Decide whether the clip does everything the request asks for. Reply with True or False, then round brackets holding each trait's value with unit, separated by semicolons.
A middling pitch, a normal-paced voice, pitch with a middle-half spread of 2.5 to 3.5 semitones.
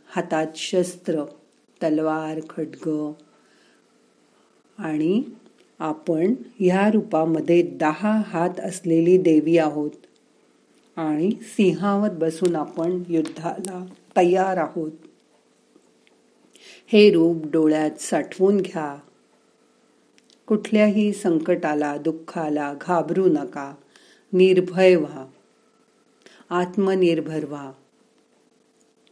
False (170 Hz; 70 wpm; 3.2 semitones)